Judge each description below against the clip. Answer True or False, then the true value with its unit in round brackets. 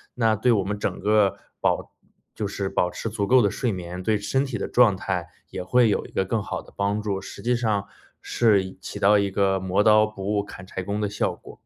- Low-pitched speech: True (100 Hz)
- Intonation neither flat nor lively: False (2.1 semitones)